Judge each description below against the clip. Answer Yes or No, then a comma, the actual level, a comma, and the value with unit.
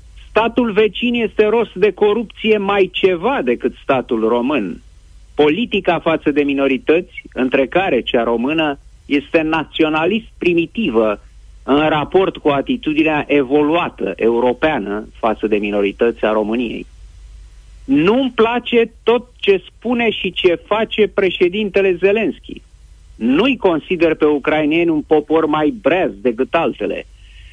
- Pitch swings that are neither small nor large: No, wide, 8.1 semitones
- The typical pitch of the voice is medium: Yes, medium, 160 Hz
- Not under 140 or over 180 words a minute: No, slow, 115 wpm